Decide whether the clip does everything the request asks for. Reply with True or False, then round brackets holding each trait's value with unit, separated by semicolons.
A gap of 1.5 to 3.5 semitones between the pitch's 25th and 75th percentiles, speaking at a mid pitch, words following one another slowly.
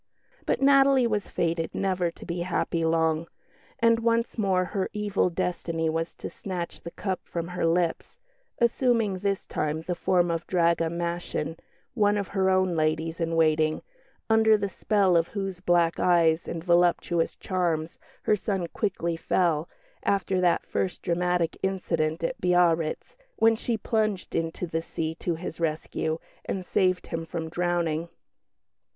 False (2.8 semitones; 175 Hz; 150 wpm)